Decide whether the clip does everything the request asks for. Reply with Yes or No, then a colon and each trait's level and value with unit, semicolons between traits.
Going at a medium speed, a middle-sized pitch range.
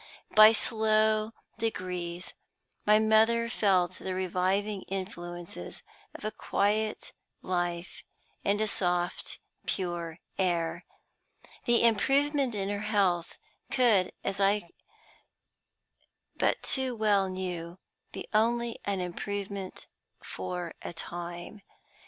No: slow, 100 wpm; average, 3.4 semitones